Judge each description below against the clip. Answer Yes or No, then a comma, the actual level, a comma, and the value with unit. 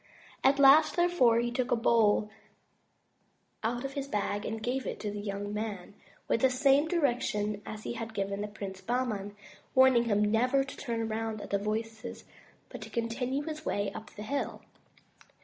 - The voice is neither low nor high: No, high, 230 Hz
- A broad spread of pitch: No, average, 3.9 semitones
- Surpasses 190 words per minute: No, average, 175 wpm